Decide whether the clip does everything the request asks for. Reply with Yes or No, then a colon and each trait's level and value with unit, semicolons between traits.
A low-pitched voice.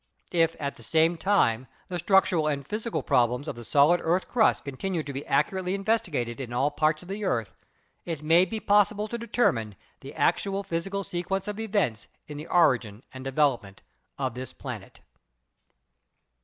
No: medium, 165 Hz